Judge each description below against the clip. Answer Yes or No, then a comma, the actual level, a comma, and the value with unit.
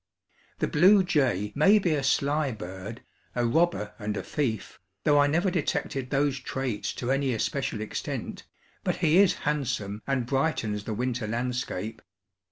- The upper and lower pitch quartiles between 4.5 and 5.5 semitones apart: Yes, average, 5.2 semitones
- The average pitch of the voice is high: No, low, 135 Hz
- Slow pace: No, average, 155 wpm